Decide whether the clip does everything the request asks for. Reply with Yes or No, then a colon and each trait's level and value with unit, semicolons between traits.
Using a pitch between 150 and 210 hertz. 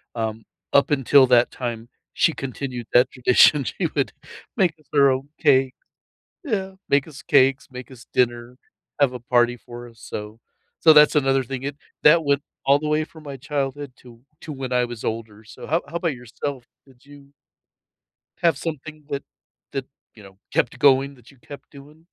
No: low, 135 Hz